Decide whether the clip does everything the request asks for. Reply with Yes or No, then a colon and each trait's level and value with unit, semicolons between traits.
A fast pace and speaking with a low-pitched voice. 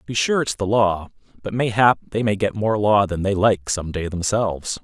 Yes: fast, 235 wpm; low, 100 Hz